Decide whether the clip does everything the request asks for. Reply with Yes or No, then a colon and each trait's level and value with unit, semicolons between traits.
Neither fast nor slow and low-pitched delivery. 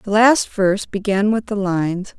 No: average, 190 wpm; high, 200 Hz